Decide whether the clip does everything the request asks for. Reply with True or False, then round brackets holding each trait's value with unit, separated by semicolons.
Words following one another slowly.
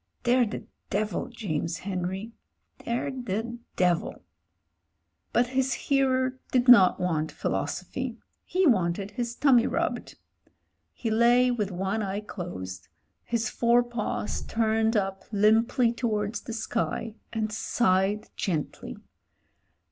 True (115 wpm)